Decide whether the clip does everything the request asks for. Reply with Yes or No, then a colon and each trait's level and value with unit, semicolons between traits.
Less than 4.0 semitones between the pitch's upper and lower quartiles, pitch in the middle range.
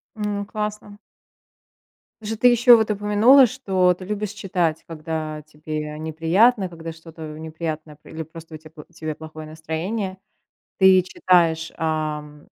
No: average, 4.7 semitones; medium, 165 Hz